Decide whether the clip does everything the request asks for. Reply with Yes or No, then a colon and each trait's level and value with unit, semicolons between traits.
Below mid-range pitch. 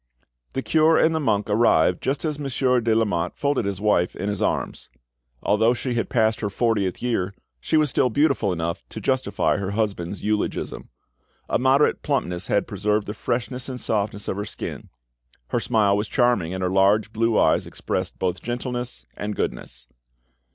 Yes: low, 110 Hz